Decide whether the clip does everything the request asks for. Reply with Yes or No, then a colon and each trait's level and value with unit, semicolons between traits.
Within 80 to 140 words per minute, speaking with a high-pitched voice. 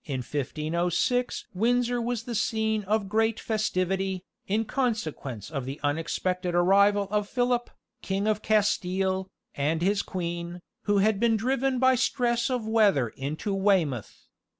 Yes: slow, 135 wpm; high, 200 Hz